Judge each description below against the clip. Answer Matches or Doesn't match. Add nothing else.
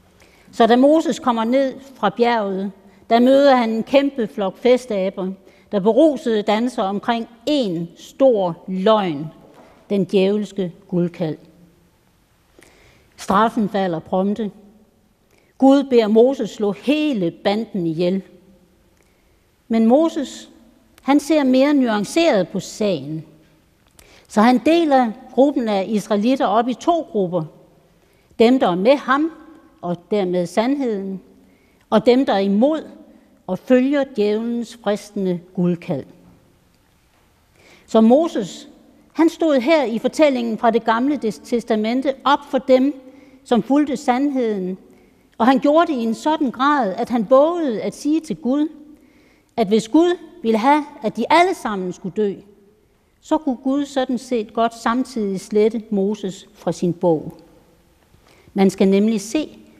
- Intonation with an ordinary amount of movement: Doesn't match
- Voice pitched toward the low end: Doesn't match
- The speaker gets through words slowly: Matches